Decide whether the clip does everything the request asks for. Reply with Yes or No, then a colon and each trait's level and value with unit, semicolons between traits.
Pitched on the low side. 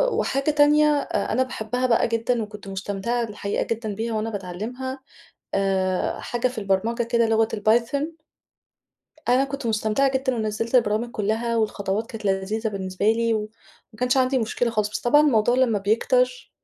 No: high, 225 Hz